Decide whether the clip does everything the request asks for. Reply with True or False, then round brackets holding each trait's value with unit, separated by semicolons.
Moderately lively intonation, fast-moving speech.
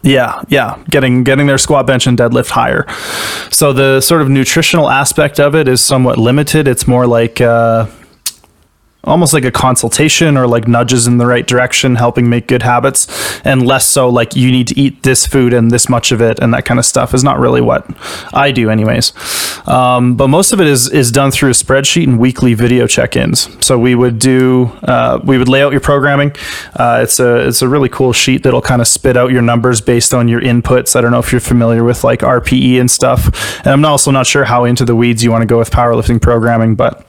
False (2.2 semitones; 225 wpm)